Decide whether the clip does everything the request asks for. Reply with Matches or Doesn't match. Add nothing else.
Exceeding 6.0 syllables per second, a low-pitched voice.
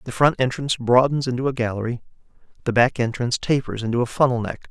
Matches